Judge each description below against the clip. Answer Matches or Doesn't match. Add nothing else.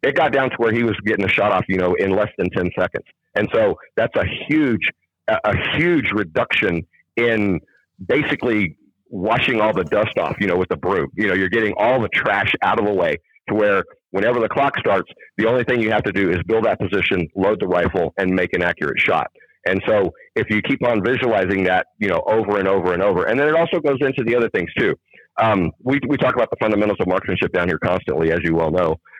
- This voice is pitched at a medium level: Doesn't match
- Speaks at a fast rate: Matches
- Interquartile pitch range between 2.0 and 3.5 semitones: Doesn't match